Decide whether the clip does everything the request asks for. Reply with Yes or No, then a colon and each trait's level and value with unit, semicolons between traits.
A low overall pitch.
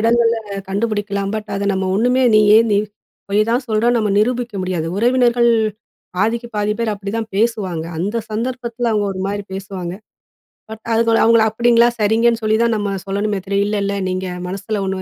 No: high, 215 Hz